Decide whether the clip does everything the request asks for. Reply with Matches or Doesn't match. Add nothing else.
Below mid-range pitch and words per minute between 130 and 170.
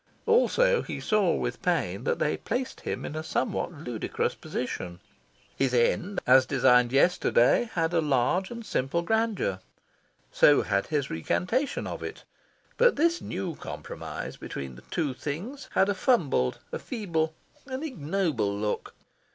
Doesn't match